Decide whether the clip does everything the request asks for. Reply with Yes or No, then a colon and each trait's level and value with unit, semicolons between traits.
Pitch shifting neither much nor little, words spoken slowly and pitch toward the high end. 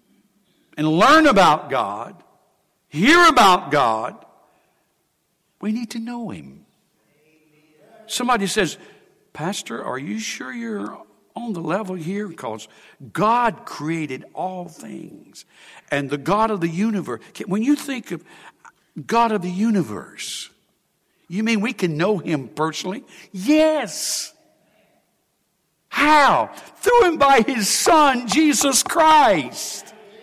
No: wide, 6.4 semitones; slow, 115 wpm; high, 210 Hz